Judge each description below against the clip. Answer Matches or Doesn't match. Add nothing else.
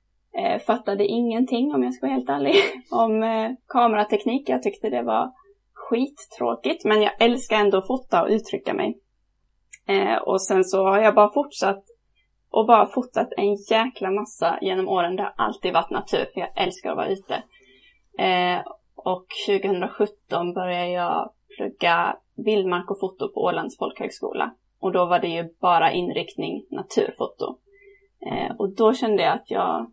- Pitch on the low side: Doesn't match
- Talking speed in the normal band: Matches